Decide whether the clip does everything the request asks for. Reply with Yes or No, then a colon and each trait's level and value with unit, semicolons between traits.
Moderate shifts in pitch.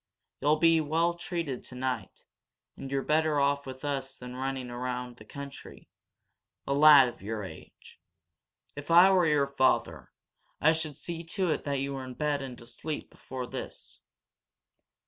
Yes: average, 3.3 semitones